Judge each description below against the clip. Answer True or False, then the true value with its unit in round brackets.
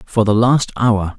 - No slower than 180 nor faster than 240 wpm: True (205 wpm)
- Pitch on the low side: True (110 Hz)